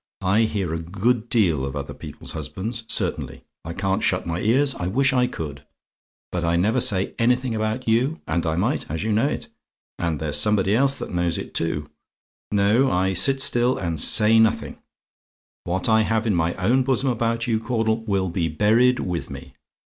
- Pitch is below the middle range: Yes, low, 105 Hz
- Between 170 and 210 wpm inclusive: Yes, average, 190 wpm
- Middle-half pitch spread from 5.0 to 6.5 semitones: Yes, average, 5.3 semitones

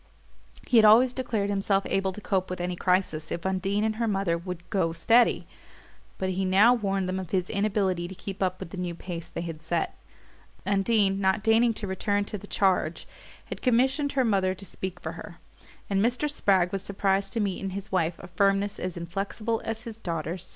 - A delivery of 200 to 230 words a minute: Yes, fast, 205 wpm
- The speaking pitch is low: No, high, 195 Hz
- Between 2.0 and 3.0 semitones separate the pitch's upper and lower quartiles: Yes, average, 2.7 semitones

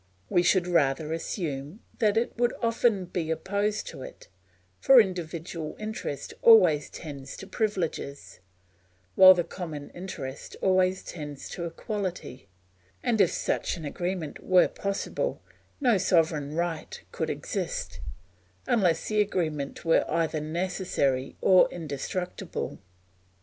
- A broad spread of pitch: No, average, 4.3 semitones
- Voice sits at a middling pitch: Yes, medium, 175 Hz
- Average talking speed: No, slow, 120 wpm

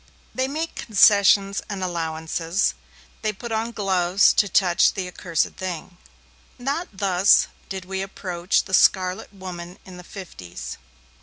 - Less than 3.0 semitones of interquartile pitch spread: Yes, narrow, 2.4 semitones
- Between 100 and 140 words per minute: Yes, slow, 135 wpm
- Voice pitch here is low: No, high, 190 Hz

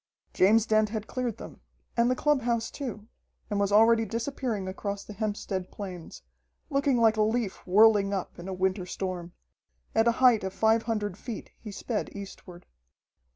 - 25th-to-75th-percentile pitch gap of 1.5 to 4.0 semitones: Yes, average, 2.9 semitones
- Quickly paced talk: No, average, 165 wpm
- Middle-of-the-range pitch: No, high, 215 Hz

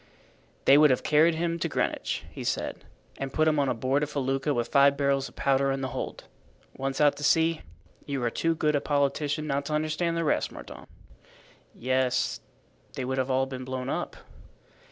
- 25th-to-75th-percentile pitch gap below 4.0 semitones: Yes, narrow, 2.4 semitones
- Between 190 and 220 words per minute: Yes, average, 195 wpm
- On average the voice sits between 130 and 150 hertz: Yes, medium, 140 Hz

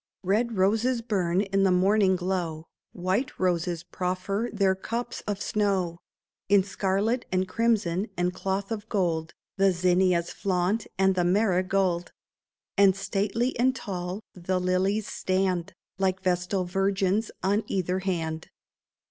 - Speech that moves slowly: Yes, slow, 130 wpm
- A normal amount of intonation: No, narrow, 2.0 semitones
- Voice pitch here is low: No, high, 190 Hz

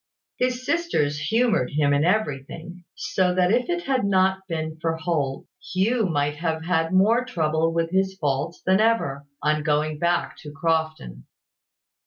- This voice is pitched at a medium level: Yes, medium, 165 Hz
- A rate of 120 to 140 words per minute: No, average, 155 wpm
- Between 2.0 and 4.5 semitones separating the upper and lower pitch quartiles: Yes, average, 4.1 semitones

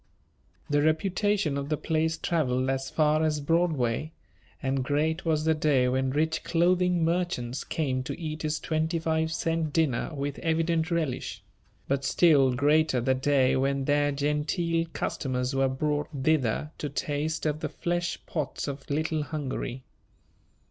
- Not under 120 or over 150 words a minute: Yes, average, 145 wpm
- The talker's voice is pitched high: No, medium, 150 Hz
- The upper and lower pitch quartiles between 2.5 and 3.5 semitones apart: Yes, average, 2.9 semitones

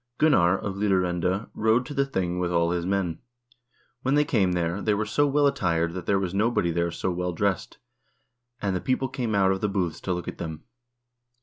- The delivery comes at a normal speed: No, fast, 210 wpm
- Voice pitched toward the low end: Yes, very low, 95 Hz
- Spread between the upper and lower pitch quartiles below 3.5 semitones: No, average, 4.0 semitones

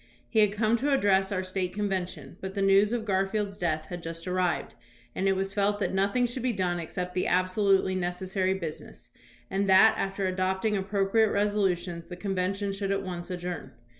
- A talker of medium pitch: No, high, 195 Hz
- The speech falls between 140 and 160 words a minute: No, average, 195 wpm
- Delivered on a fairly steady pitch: Yes, narrow, 1.9 semitones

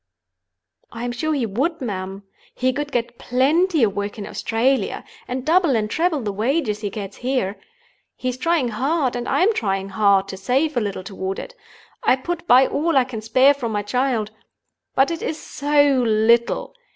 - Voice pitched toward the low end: No, very high, 250 Hz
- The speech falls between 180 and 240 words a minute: Yes, average, 185 wpm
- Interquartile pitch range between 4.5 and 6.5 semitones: Yes, average, 5.2 semitones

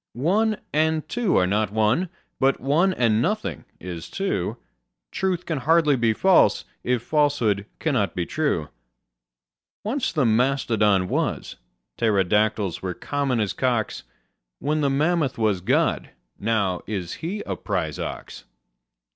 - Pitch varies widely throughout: Yes, wide, 7.1 semitones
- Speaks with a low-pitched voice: Yes, low, 125 Hz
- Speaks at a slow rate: Yes, slow, 130 wpm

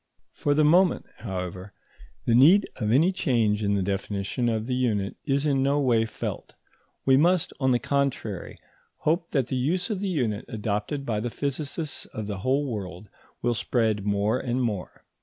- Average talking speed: Yes, average, 175 wpm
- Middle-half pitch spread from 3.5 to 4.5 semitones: No, wide, 5.4 semitones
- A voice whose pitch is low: Yes, low, 120 Hz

